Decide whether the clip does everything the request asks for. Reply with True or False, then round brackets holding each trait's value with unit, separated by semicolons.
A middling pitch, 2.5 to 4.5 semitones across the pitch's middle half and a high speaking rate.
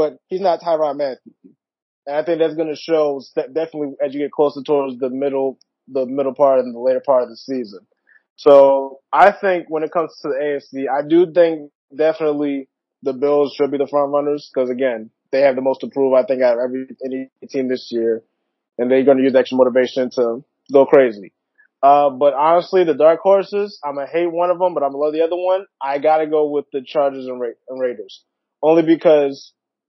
True (145 Hz; 3.1 semitones; 220 wpm)